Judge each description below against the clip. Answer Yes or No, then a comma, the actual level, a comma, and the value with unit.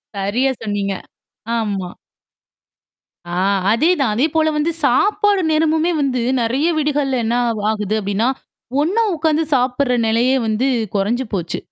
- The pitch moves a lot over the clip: Yes, wide, 6.1 semitones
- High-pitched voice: Yes, very high, 255 Hz